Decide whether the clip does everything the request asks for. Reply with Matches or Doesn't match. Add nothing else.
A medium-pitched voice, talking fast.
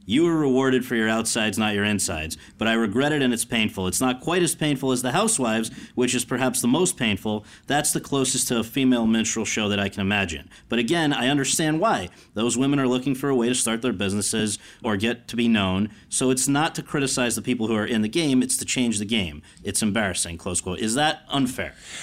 Doesn't match